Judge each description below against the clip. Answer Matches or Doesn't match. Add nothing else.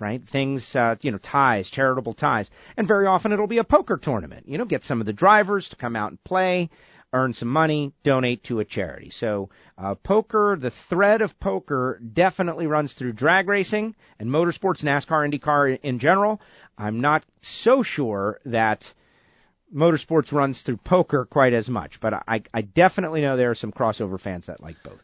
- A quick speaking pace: Doesn't match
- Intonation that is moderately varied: Doesn't match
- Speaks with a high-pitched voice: Doesn't match